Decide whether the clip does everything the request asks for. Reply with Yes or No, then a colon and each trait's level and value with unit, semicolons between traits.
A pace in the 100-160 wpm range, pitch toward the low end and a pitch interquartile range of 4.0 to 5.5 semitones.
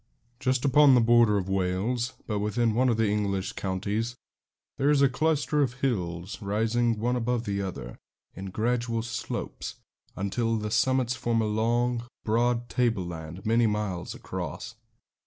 No: average, 150 wpm; low, 115 Hz; average, 3.2 semitones